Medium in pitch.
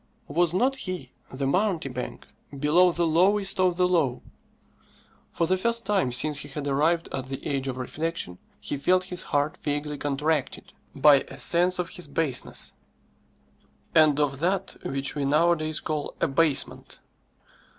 Yes: medium, 155 Hz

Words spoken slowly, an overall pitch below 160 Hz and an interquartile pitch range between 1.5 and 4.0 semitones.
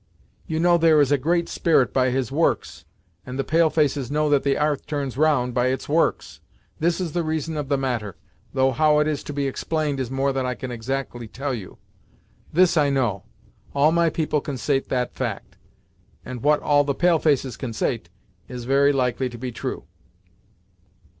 No: average, 190 wpm; medium, 140 Hz; average, 3.2 semitones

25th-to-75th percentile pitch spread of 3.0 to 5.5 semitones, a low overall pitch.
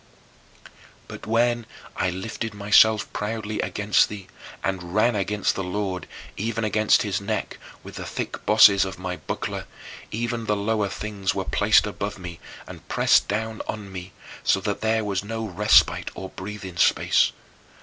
No: narrow, 2.4 semitones; low, 105 Hz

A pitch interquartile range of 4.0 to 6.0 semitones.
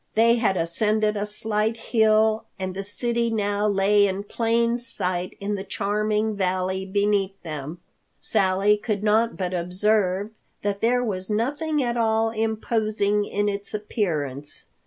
No: narrow, 2.4 semitones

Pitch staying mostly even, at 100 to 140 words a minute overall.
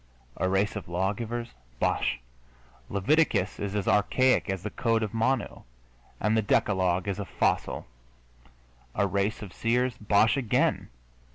No: average, 3.0 semitones; slow, 135 wpm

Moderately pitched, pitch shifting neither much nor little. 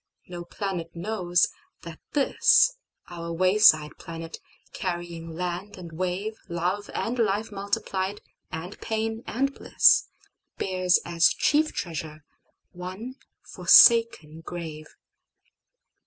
Yes: medium, 180 Hz; average, 3.8 semitones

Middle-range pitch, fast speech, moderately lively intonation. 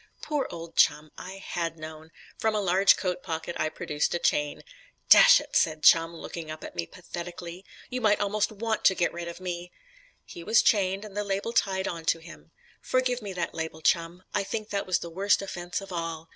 Yes: medium, 180 Hz; fast, 210 wpm; average, 3.3 semitones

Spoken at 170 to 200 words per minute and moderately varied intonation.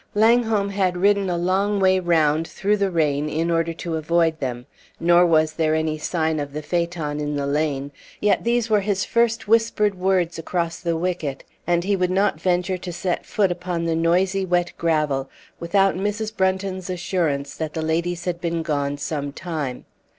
Yes: average, 180 wpm; average, 3.3 semitones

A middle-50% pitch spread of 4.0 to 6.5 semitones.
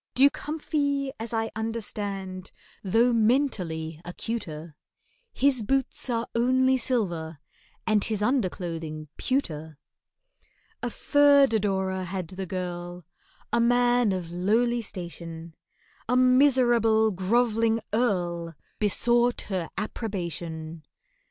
Yes: wide, 5.6 semitones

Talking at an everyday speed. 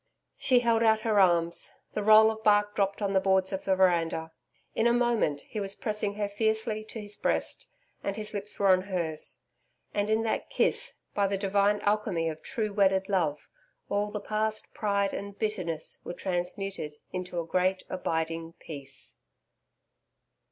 Yes: average, 170 wpm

